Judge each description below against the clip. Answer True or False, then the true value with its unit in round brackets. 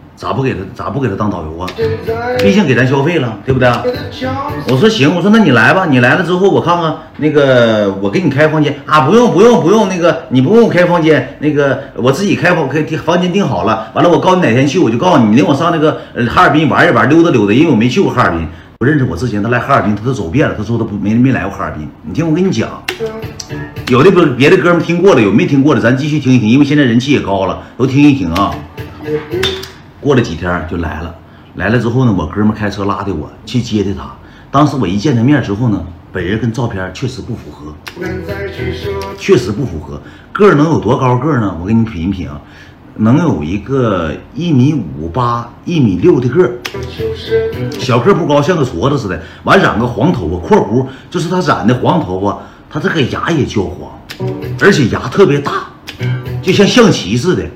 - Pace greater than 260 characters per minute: True (315 characters per minute)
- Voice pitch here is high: False (125 Hz)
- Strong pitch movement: True (7.1 semitones)